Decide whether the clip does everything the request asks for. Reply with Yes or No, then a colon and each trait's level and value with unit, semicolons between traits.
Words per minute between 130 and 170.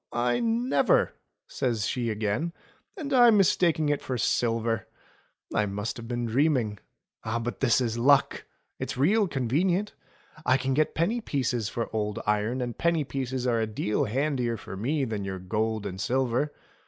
Yes: average, 160 wpm